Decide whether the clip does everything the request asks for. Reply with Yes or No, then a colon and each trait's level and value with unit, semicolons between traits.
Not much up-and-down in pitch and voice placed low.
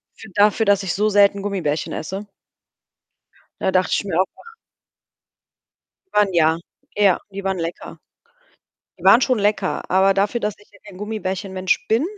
No: narrow, 1.8 semitones; high, 200 Hz